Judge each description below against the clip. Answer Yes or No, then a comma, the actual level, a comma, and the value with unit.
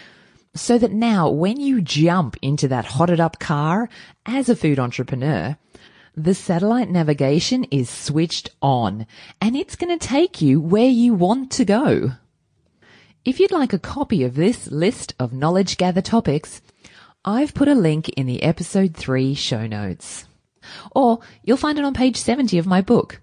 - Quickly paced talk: No, average, 165 wpm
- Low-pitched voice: No, medium, 180 Hz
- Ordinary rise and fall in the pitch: No, wide, 8.9 semitones